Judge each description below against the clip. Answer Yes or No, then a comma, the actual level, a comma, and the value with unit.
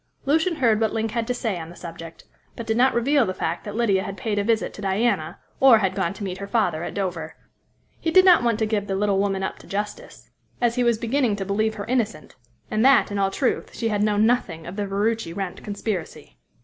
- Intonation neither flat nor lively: Yes, average, 3.3 semitones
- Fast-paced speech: Yes, fast, 240 wpm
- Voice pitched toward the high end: Yes, high, 210 Hz